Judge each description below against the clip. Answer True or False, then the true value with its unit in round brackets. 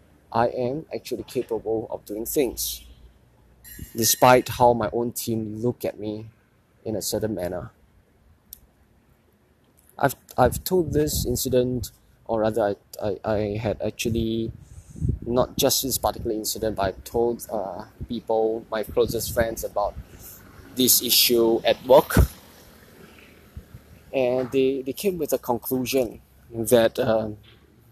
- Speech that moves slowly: True (125 wpm)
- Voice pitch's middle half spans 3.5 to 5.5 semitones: False (2.5 semitones)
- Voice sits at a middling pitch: False (115 Hz)